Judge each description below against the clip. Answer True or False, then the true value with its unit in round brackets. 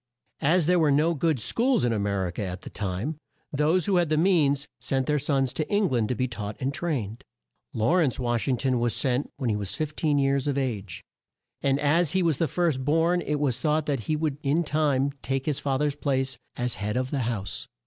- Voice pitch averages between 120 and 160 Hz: True (140 Hz)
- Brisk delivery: True (230 wpm)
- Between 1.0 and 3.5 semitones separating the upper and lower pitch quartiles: False (4.0 semitones)